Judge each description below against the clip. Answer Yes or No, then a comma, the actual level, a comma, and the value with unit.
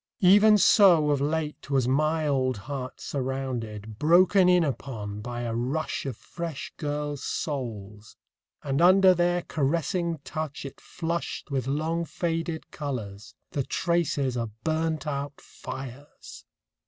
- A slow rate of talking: Yes, slow, 130 wpm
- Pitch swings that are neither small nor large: Yes, average, 4.3 semitones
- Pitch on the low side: No, medium, 145 Hz